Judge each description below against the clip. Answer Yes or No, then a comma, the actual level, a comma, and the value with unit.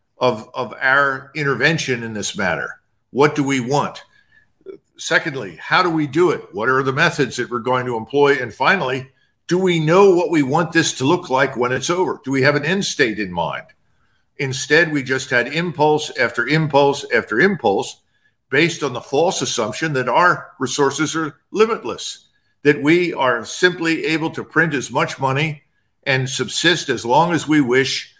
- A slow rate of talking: No, average, 180 wpm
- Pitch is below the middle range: No, medium, 145 Hz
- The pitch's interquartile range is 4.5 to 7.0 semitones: No, average, 3.9 semitones